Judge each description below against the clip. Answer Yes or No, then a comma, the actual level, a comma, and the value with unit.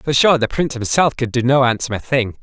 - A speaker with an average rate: No, fast, 245 wpm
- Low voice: Yes, low, 130 Hz